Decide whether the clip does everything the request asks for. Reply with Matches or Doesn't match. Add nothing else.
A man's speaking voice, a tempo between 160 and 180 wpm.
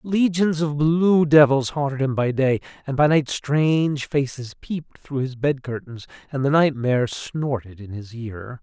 Matches